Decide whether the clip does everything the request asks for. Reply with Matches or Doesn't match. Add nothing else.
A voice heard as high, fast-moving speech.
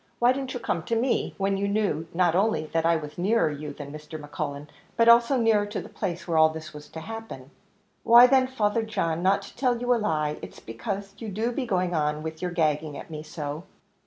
Doesn't match